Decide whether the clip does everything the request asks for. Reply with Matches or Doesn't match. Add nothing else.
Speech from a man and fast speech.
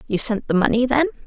Doesn't match